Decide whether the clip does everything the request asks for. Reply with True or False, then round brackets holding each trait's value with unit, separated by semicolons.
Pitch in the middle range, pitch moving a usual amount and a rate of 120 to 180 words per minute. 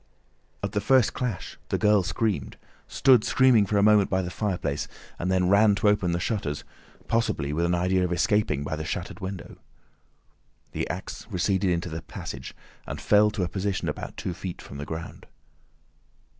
False (95 Hz; 3.3 semitones; 175 wpm)